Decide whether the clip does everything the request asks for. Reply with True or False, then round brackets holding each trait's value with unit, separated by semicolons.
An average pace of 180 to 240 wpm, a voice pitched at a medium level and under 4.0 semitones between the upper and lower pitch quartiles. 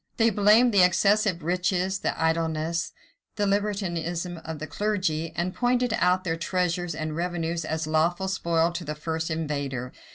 False (155 wpm; 170 Hz; 2.9 semitones)